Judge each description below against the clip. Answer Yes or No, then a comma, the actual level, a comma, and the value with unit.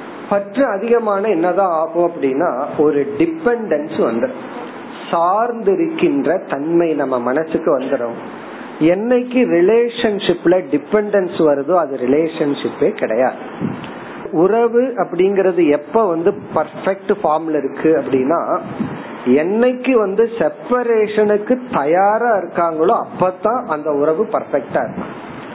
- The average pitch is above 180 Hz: Yes, high, 190 Hz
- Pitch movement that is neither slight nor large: No, wide, 6.2 semitones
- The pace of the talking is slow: Yes, slow, 65 wpm